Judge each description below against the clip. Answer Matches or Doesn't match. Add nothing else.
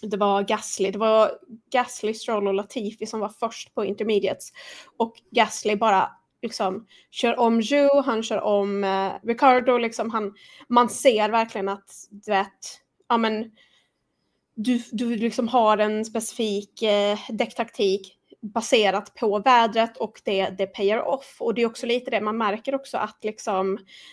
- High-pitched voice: Matches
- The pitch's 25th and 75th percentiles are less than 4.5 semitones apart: Matches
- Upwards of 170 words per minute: Doesn't match